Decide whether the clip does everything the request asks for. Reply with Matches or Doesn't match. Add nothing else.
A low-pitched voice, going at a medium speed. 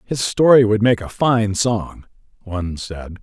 Matches